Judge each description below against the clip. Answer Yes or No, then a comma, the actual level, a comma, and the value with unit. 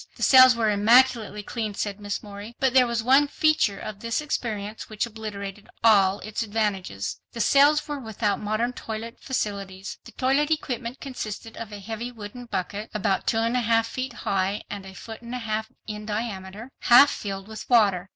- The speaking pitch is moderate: No, high, 220 Hz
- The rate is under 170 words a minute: No, average, 185 wpm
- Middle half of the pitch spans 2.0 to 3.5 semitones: Yes, average, 3.0 semitones